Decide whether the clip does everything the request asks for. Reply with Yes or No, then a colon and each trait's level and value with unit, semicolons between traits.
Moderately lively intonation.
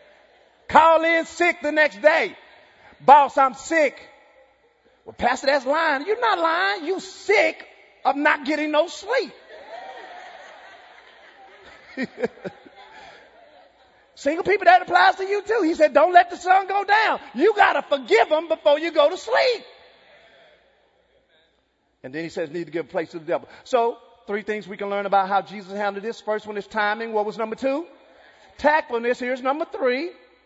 No: wide, 7.1 semitones